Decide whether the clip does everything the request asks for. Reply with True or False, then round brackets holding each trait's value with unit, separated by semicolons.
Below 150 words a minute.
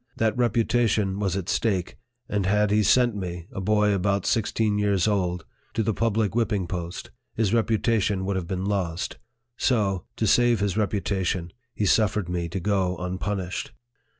False (160 wpm)